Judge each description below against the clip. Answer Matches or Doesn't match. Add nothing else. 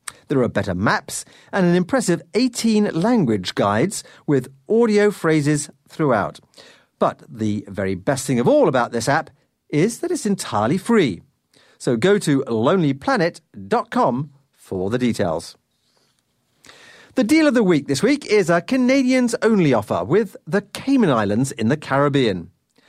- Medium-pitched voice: Matches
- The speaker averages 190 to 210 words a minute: Doesn't match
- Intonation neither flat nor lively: Doesn't match